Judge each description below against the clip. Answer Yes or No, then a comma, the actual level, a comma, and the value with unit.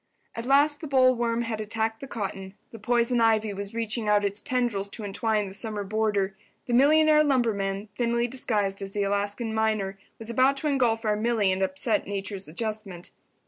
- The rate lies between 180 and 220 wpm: No, average, 170 wpm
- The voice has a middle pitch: No, high, 220 Hz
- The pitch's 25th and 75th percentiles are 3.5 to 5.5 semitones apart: No, average, 2.9 semitones